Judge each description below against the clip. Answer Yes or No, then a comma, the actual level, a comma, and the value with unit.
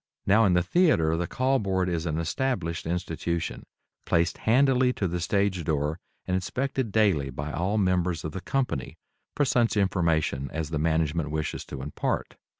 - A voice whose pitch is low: Yes, very low, 90 Hz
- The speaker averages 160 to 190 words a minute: Yes, average, 165 wpm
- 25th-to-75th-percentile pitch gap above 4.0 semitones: Yes, average, 4.6 semitones